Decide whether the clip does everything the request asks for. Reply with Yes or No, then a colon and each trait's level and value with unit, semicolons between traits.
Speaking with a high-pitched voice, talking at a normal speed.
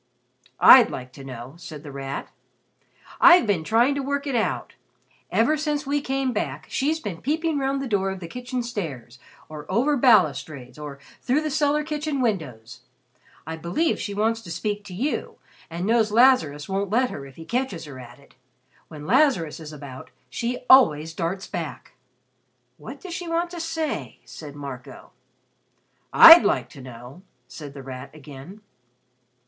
Yes: high, 195 Hz; average, 165 wpm